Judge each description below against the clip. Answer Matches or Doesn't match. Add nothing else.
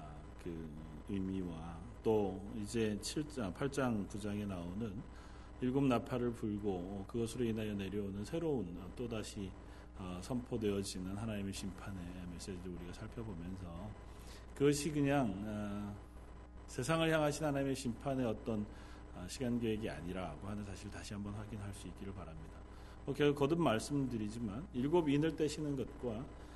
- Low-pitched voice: Matches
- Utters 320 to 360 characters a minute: Doesn't match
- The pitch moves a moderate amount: Matches